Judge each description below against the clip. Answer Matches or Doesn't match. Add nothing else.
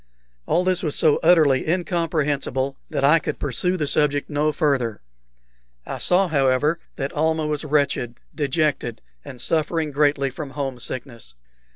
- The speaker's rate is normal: Matches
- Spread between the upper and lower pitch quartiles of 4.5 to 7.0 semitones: Doesn't match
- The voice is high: Doesn't match